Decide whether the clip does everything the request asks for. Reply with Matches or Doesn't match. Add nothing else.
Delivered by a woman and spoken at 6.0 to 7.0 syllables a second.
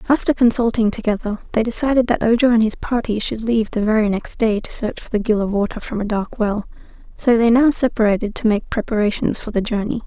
Matches